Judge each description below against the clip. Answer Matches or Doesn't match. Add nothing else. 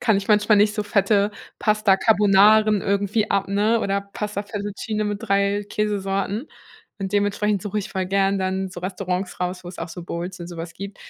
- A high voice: Matches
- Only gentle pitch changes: Matches